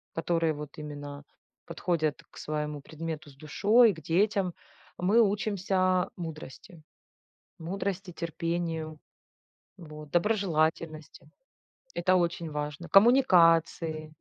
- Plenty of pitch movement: No, average, 3.2 semitones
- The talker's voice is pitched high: No, medium, 165 Hz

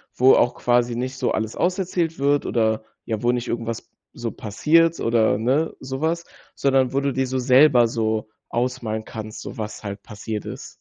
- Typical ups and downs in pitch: Yes, average, 3.5 semitones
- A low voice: Yes, low, 120 Hz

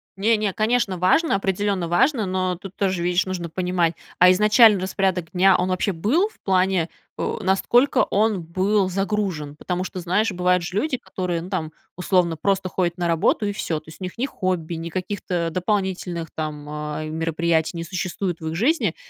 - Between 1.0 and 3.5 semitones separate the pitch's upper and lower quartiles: Yes, average, 2.7 semitones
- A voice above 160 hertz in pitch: Yes, medium, 185 Hz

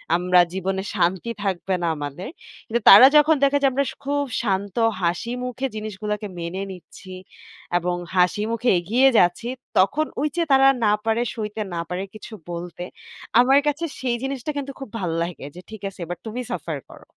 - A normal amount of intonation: No, wide, 5.9 semitones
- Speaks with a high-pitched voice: Yes, high, 210 Hz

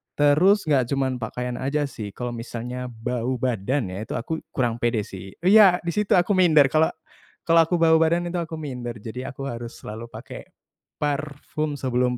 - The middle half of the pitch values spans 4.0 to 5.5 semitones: Yes, average, 5.0 semitones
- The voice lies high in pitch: No, low, 135 Hz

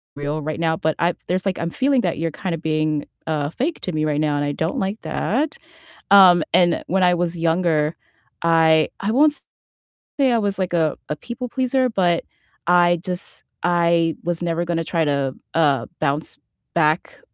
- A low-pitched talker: No, medium, 170 Hz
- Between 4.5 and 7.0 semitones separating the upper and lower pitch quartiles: No, average, 3.2 semitones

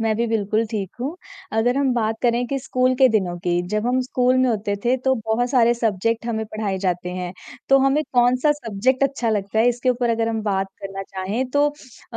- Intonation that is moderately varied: Yes, average, 3.6 semitones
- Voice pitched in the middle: No, high, 230 Hz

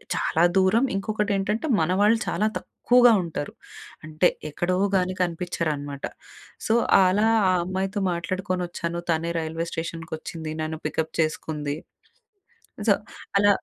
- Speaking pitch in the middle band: Yes, medium, 175 Hz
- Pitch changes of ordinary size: Yes, average, 3.4 semitones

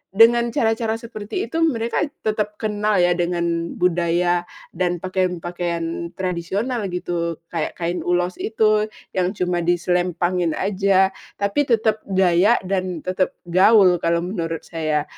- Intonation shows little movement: No, average, 3.3 semitones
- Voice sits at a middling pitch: Yes, medium, 180 Hz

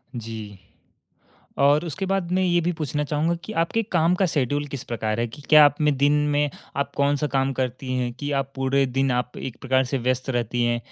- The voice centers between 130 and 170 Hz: Yes, medium, 140 Hz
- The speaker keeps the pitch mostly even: No, average, 3.2 semitones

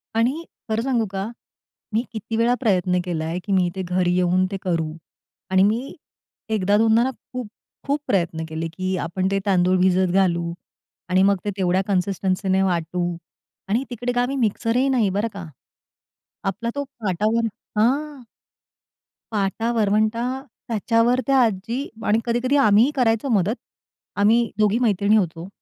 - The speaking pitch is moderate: No, high, 205 Hz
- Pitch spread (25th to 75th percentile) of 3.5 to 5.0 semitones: Yes, average, 3.9 semitones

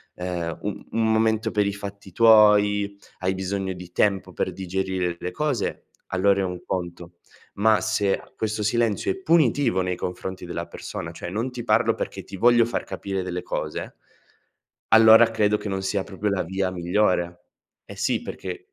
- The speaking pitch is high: No, low, 100 Hz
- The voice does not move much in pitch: No, average, 3.1 semitones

